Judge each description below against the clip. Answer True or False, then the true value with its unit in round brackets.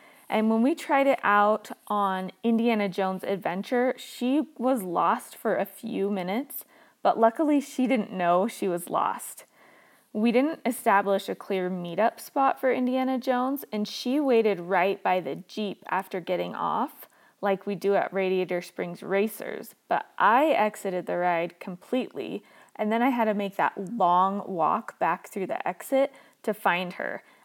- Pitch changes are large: False (5.0 semitones)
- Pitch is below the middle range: False (210 Hz)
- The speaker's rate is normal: True (160 wpm)